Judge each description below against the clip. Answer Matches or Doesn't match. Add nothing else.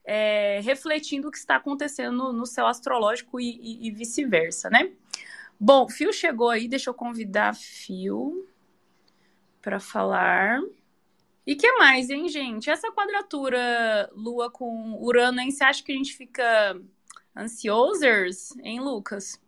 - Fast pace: Doesn't match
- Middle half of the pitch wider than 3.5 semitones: Matches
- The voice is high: Matches